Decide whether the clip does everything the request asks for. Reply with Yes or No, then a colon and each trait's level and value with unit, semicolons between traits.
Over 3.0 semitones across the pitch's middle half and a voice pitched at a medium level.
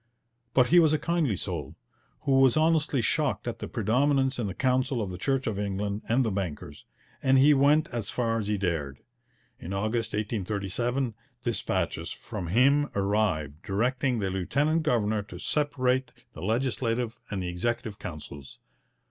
No: average, 5.2 semitones; low, 115 Hz